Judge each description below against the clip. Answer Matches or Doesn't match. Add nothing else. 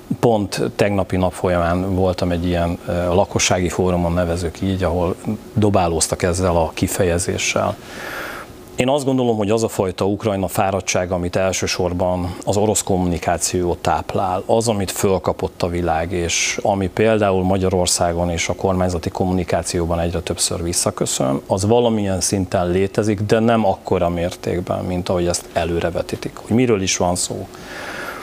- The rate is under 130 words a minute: Doesn't match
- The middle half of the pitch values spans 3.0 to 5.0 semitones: Doesn't match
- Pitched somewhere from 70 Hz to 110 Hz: Matches